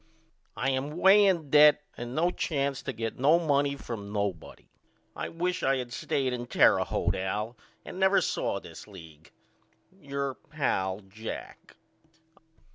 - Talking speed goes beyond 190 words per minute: No, average, 150 wpm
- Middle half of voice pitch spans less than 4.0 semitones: No, wide, 5.6 semitones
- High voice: No, low, 135 Hz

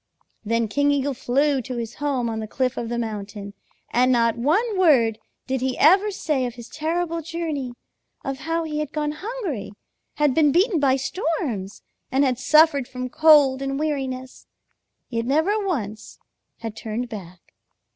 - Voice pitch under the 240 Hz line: No, very high, 270 Hz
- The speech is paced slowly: No, average, 165 wpm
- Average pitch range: Yes, average, 4.6 semitones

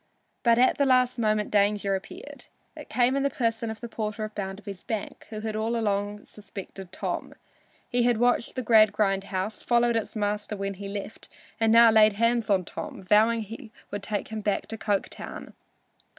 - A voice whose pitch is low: No, high, 215 Hz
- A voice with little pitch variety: Yes, narrow, 2.3 semitones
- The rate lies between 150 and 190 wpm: Yes, average, 185 wpm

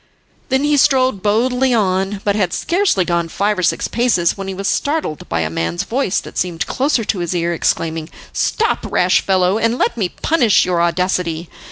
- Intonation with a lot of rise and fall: Yes, wide, 6.0 semitones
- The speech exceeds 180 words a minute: Yes, average, 190 wpm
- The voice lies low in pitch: No, high, 195 Hz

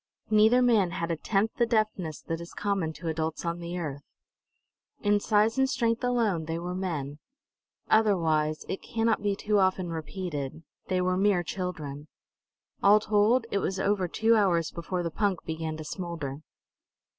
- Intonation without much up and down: No, average, 4.4 semitones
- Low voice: No, medium, 185 Hz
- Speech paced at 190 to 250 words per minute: No, average, 165 wpm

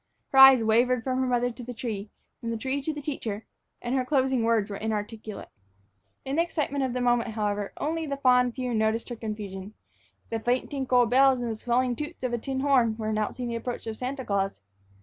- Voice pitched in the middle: No, high, 245 Hz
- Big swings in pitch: No, average, 3.0 semitones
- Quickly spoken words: Yes, fast, 220 wpm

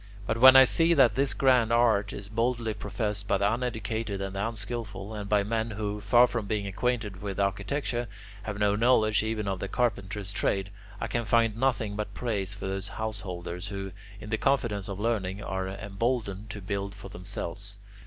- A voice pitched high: No, low, 105 Hz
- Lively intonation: No, average, 2.7 semitones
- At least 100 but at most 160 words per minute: No, average, 185 wpm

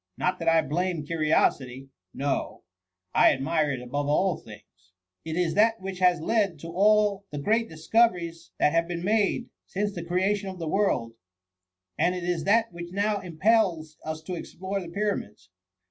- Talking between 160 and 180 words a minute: Yes, average, 175 wpm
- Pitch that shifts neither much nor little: Yes, average, 4.1 semitones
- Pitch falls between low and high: Yes, medium, 175 Hz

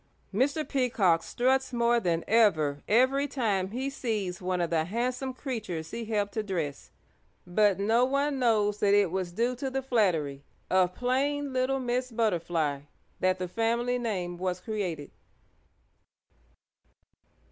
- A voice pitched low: No, high, 220 Hz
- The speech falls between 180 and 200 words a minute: No, average, 140 wpm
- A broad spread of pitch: Yes, wide, 5.7 semitones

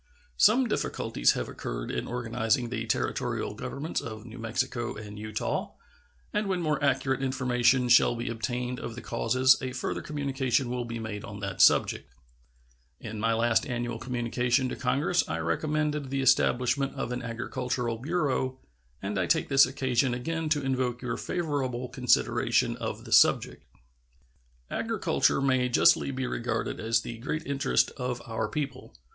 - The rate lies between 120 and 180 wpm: Yes, average, 155 wpm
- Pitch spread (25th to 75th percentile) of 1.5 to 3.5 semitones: Yes, average, 2.7 semitones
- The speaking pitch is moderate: No, low, 125 Hz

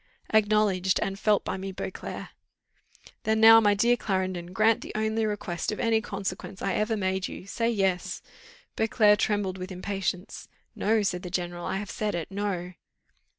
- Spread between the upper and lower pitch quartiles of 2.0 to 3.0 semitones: Yes, narrow, 2.5 semitones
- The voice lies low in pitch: No, high, 200 Hz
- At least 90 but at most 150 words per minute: No, average, 165 wpm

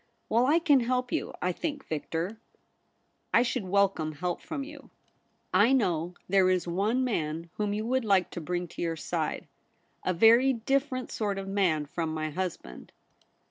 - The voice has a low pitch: No, high, 195 Hz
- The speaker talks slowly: No, average, 180 wpm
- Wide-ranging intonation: Yes, wide, 6.5 semitones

